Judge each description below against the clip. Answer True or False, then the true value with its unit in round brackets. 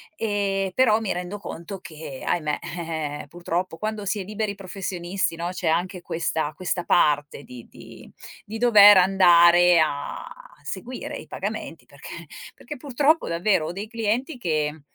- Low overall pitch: False (180 Hz)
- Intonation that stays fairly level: False (4.1 semitones)